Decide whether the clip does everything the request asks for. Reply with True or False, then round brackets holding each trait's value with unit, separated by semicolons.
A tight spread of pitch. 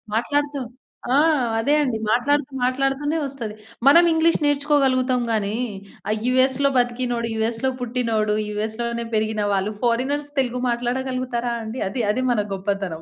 False (3.3 semitones)